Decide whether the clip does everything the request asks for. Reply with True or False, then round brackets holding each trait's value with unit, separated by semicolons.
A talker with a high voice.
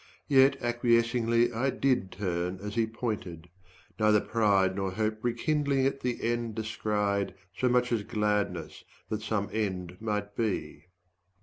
False (110 Hz)